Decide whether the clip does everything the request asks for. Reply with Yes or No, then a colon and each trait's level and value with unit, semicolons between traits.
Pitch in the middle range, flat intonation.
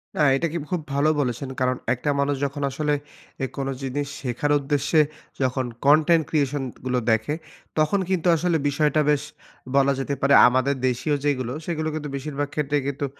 Yes: medium, 145 Hz; narrow, 2.2 semitones